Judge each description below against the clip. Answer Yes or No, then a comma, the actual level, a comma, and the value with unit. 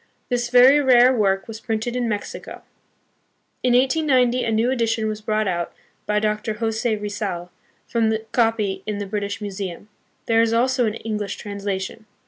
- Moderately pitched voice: No, high, 220 Hz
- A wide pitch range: No, narrow, 2.6 semitones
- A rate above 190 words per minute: No, average, 160 wpm